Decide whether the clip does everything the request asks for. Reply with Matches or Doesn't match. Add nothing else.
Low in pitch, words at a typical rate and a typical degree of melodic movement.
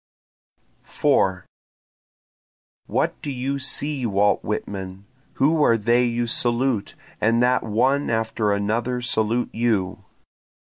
Doesn't match